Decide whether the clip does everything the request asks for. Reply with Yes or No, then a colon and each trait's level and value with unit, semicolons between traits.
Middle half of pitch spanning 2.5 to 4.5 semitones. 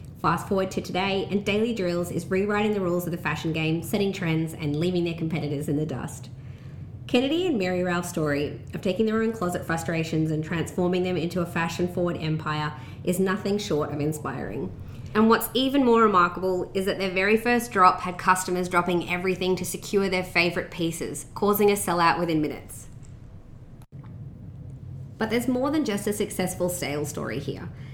Yes: average, 4.1 semitones